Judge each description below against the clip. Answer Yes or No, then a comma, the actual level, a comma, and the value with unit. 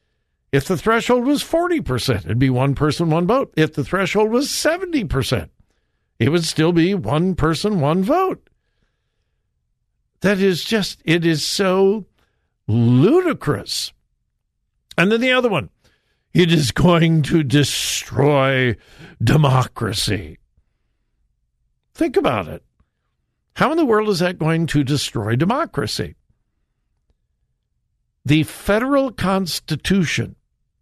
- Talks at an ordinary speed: No, slow, 115 wpm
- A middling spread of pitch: No, wide, 7.2 semitones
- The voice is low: No, medium, 165 Hz